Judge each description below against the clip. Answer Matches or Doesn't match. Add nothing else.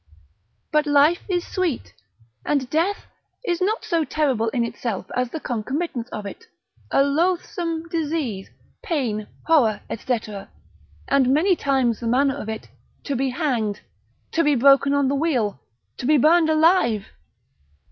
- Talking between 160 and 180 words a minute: Doesn't match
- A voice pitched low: Doesn't match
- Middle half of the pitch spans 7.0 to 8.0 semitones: Doesn't match